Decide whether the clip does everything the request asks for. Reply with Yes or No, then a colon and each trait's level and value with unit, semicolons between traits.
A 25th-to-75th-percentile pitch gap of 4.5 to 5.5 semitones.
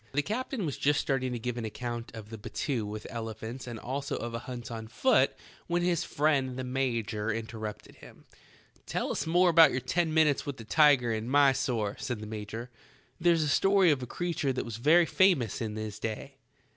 Yes: average, 5.1 semitones